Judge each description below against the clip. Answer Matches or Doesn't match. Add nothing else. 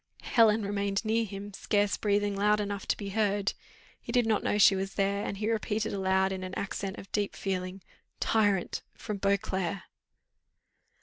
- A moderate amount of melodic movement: Doesn't match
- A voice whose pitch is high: Matches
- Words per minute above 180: Doesn't match